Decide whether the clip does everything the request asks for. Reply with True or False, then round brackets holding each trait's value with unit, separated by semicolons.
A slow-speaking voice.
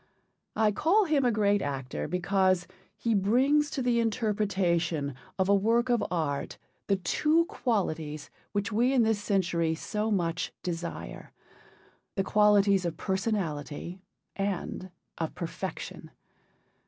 True (125 wpm)